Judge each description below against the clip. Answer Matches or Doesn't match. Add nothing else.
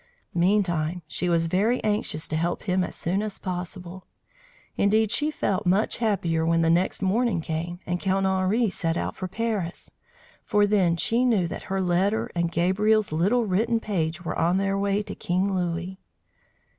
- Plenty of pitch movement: Doesn't match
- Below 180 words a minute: Matches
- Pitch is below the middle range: Doesn't match